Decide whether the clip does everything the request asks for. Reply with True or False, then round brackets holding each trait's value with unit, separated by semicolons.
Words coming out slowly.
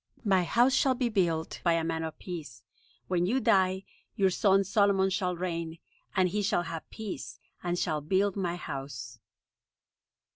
False (160 wpm)